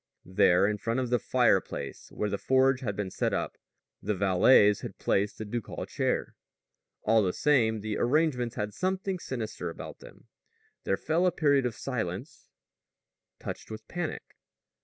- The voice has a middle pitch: No, low, 115 Hz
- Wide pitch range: No, average, 4.7 semitones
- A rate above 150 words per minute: Yes, average, 160 wpm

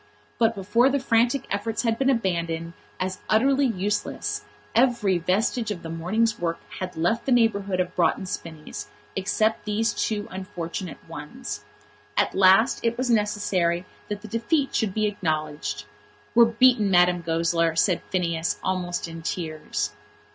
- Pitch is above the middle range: Yes, high, 195 Hz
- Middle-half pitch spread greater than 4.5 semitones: Yes, average, 5.0 semitones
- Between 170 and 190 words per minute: No, average, 145 wpm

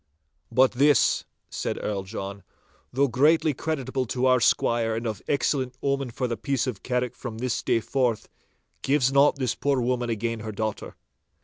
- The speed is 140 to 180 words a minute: Yes, average, 175 wpm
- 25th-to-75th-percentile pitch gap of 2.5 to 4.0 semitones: Yes, average, 3.1 semitones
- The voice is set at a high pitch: No, low, 125 Hz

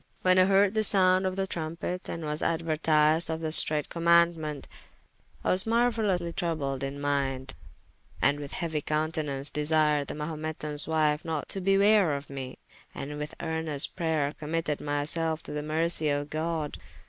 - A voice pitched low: No, medium, 155 Hz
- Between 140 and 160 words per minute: Yes, average, 155 wpm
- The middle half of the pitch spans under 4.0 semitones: Yes, narrow, 2.5 semitones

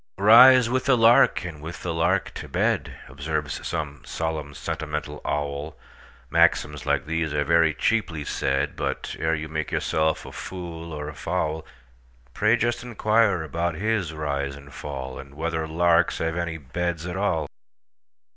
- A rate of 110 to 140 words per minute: Yes, slow, 135 wpm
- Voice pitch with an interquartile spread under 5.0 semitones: Yes, average, 3.1 semitones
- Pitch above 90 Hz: No, very low, 80 Hz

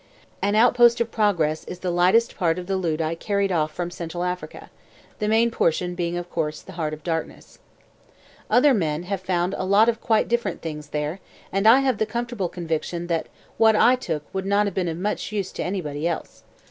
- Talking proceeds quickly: Yes, fast, 210 wpm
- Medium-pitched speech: Yes, medium, 180 Hz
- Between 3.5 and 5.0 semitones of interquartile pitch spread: Yes, average, 4.2 semitones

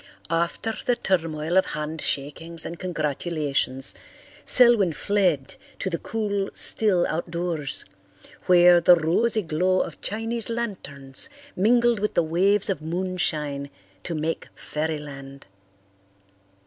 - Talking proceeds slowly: Yes, slow, 110 wpm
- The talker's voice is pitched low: No, medium, 170 Hz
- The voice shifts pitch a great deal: No, average, 4.5 semitones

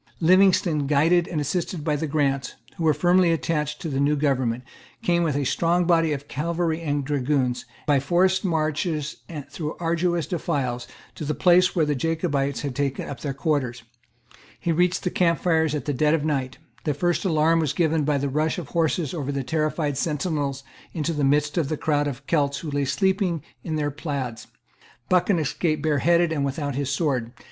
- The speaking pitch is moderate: Yes, medium, 150 Hz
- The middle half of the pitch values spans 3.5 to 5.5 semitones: No, average, 2.9 semitones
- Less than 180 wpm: No, average, 190 wpm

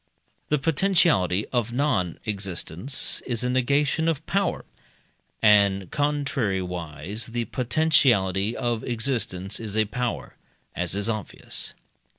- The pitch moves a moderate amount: No, wide, 6.1 semitones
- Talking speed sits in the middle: No, slow, 110 wpm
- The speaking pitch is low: Yes, low, 115 Hz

